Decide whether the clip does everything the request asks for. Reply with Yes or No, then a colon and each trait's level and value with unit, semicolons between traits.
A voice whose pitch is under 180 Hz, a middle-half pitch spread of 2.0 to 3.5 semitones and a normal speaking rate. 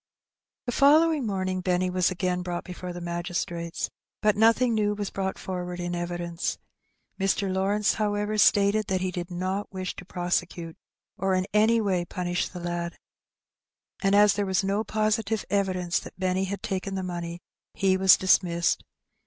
No: medium, 185 Hz; narrow, 2.5 semitones; average, 160 wpm